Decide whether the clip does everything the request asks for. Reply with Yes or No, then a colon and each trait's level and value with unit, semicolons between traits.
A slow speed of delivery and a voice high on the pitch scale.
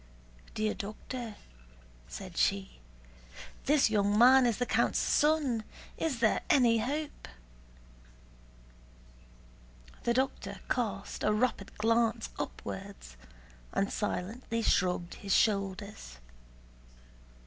Yes: slow, 95 wpm; high, 220 Hz